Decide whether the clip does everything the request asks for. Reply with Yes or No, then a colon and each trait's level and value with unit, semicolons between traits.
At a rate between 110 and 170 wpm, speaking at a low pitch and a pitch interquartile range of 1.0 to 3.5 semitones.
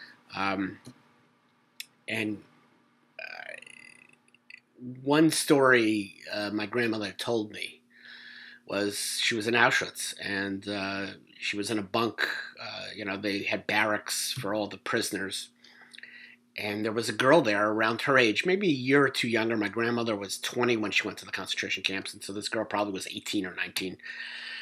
Yes: average, 165 wpm; low, 105 Hz; average, 2.9 semitones